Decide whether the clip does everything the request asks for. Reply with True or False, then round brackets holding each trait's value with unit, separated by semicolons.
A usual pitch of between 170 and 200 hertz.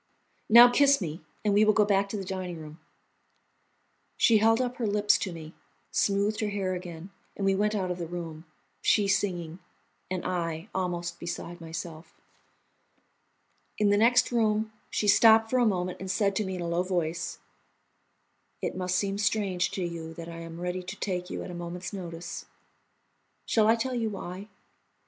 True (190 Hz)